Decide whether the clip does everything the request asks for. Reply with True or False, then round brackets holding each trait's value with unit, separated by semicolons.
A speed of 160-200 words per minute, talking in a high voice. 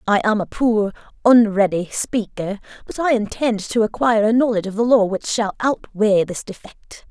True (175 wpm; 215 Hz)